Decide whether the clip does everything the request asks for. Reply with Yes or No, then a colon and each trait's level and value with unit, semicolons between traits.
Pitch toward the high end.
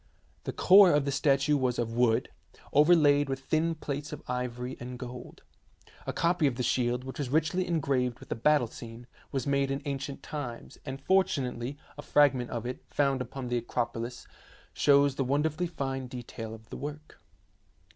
No: low, 135 Hz